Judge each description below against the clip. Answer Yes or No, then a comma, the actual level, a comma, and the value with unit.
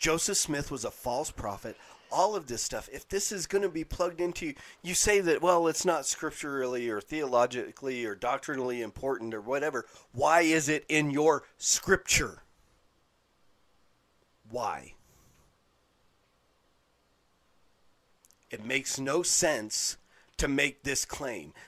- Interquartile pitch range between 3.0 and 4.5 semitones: No, average, 5.1 semitones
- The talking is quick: No, slow, 135 wpm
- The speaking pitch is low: No, medium, 150 Hz